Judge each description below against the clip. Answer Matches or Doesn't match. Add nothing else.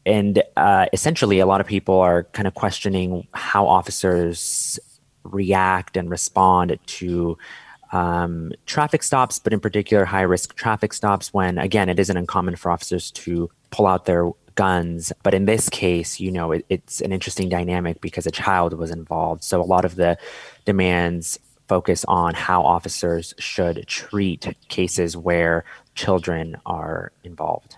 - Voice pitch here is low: Matches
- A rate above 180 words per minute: Doesn't match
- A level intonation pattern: Matches